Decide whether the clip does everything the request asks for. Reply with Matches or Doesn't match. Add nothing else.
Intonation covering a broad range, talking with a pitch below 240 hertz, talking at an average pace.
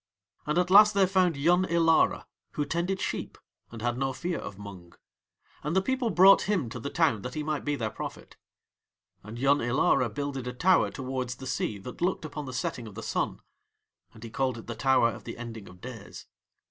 Doesn't match